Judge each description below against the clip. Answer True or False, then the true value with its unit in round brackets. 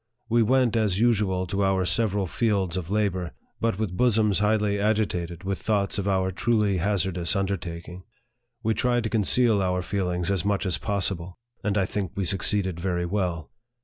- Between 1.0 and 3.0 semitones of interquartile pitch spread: True (2.6 semitones)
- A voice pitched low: True (100 Hz)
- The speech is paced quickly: False (175 wpm)